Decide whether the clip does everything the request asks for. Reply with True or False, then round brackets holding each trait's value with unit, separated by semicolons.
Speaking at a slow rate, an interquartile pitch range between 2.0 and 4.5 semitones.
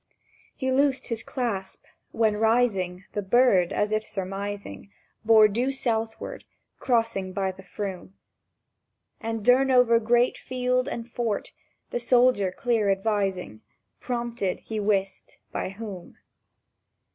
True (115 wpm; 3.8 semitones)